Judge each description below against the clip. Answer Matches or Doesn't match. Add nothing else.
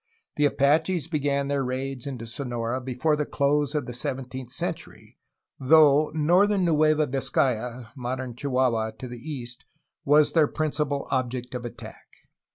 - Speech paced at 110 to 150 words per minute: Matches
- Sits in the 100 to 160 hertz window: Matches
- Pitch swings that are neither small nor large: Matches